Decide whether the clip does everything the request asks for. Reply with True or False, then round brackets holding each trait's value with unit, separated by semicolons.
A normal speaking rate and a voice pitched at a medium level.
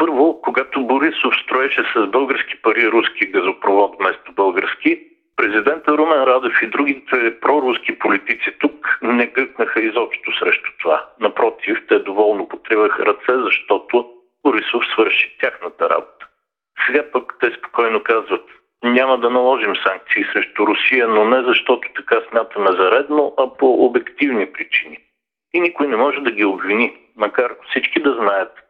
True (140 wpm; 155 Hz)